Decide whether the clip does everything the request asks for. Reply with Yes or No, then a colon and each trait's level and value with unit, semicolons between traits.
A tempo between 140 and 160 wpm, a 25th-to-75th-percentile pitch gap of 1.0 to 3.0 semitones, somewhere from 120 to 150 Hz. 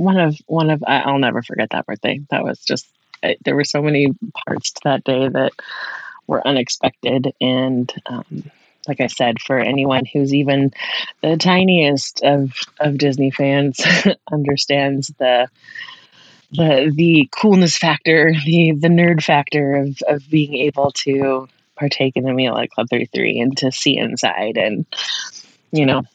Yes: average, 155 wpm; narrow, 2.6 semitones; medium, 140 Hz